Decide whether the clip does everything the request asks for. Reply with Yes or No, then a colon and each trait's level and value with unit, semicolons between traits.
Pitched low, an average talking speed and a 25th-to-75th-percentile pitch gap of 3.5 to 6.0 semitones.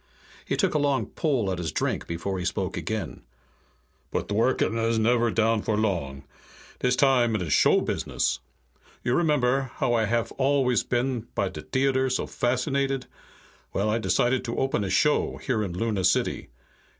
Yes: low, 120 Hz; average, 170 wpm; average, 4.0 semitones